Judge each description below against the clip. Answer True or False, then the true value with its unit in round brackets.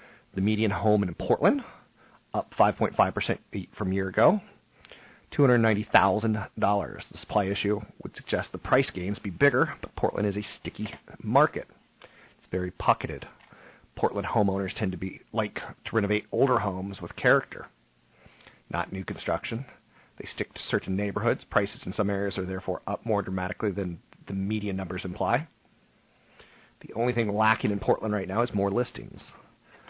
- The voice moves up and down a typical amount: False (2.3 semitones)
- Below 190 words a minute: True (170 wpm)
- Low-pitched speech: True (100 Hz)